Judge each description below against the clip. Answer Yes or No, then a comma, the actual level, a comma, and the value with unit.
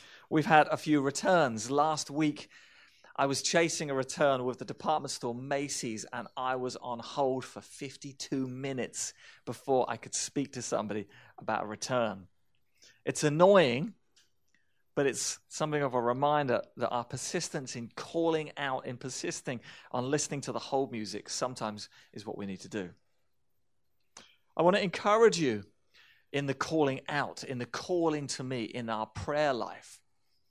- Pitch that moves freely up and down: No, average, 3.7 semitones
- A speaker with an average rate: Yes, average, 160 wpm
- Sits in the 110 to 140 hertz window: Yes, low, 135 Hz